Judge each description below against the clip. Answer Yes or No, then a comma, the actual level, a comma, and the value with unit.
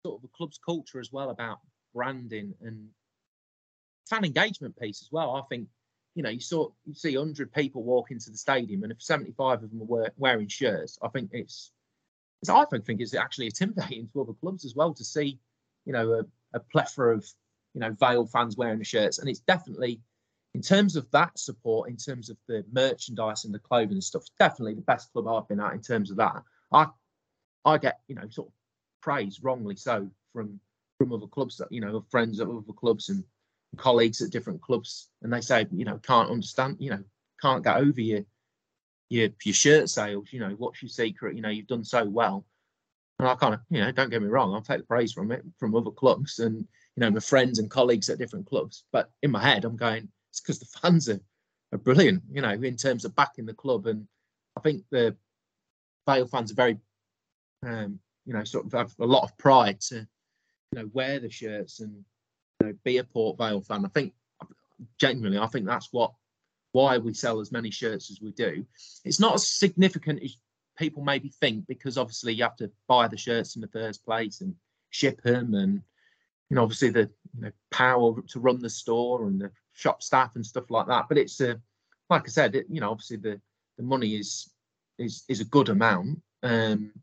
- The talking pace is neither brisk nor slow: No, fast, 215 wpm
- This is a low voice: Yes, low, 120 Hz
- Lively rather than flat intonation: No, average, 3.8 semitones